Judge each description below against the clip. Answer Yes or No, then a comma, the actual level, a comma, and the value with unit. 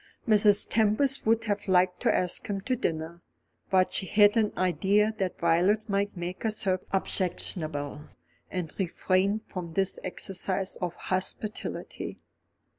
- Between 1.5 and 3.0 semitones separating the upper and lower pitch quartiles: Yes, narrow, 2.5 semitones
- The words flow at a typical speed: No, slow, 130 wpm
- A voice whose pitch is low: No, high, 190 Hz